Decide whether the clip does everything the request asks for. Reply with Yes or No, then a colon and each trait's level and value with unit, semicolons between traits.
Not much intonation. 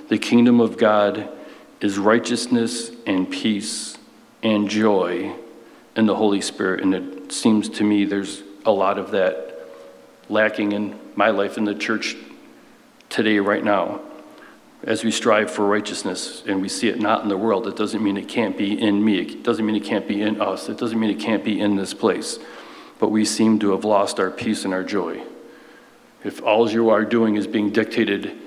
Yes: narrow, 1.7 semitones